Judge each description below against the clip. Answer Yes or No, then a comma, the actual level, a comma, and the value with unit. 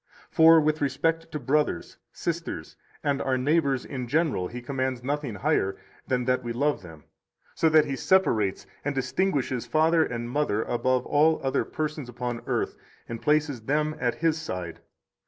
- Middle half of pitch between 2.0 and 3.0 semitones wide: No, average, 4.1 semitones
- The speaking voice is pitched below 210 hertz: Yes, low, 135 Hz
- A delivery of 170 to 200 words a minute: No, average, 160 wpm